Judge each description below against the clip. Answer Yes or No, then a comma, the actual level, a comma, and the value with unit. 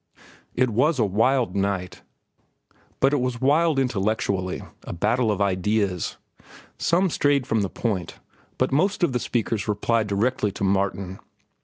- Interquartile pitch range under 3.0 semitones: No, average, 4.8 semitones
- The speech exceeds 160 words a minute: No, average, 140 wpm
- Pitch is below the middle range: Yes, low, 110 Hz